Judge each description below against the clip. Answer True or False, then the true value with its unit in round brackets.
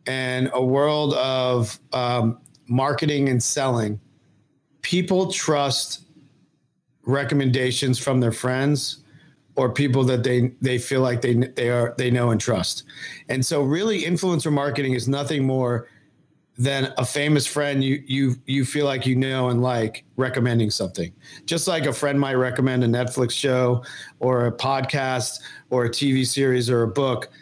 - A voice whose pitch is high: False (130 Hz)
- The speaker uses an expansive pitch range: False (2.4 semitones)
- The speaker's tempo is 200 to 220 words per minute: False (155 wpm)